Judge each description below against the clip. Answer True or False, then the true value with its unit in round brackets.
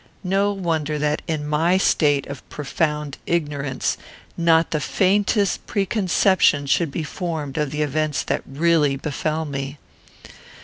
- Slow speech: True (130 wpm)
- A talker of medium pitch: True (155 Hz)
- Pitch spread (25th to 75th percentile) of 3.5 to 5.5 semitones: False (2.8 semitones)